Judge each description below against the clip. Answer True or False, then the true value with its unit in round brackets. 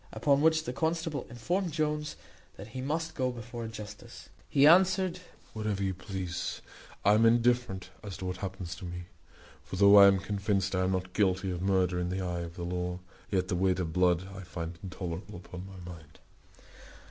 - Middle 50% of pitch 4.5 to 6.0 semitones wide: True (5.1 semitones)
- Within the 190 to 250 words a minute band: True (195 wpm)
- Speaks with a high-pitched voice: False (95 Hz)